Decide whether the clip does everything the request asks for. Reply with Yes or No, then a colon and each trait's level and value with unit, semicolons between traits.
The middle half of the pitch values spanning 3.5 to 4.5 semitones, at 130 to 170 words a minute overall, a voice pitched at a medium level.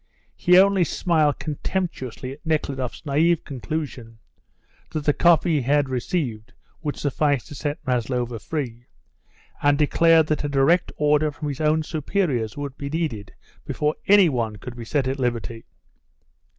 Yes: average, 3.9 semitones; average, 150 wpm; medium, 145 Hz